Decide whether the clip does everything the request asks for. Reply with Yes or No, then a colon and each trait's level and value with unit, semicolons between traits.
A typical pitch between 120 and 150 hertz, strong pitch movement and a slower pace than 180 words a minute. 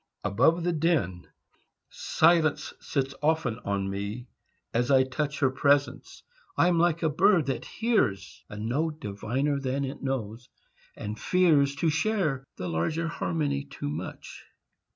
Yes: medium, 140 Hz; wide, 5.9 semitones; average, 140 wpm